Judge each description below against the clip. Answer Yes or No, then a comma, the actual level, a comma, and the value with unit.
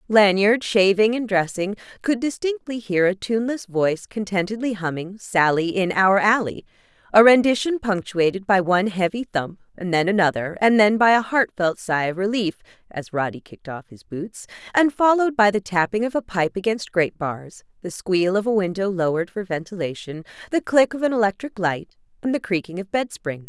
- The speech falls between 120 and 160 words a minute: No, average, 175 wpm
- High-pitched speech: Yes, high, 200 Hz